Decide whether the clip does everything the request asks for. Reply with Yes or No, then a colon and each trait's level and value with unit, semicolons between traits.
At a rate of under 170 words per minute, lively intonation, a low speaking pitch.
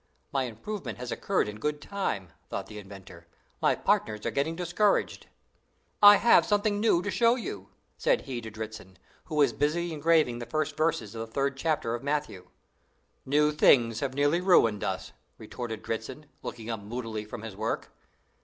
No: average, 175 wpm; wide, 6.3 semitones; low, 130 Hz